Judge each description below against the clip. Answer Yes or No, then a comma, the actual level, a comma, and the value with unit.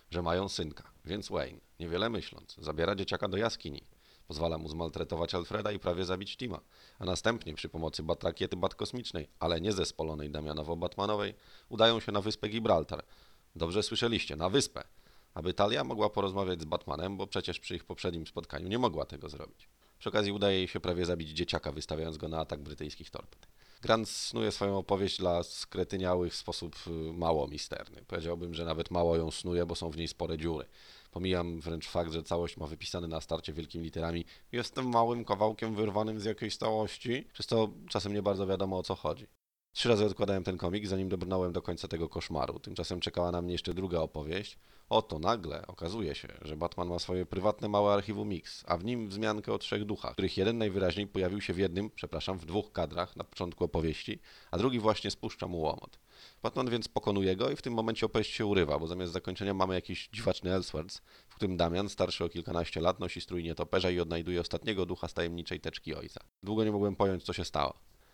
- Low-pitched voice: Yes, very low, 90 Hz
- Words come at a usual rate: No, fast, 190 wpm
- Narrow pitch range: No, average, 3.5 semitones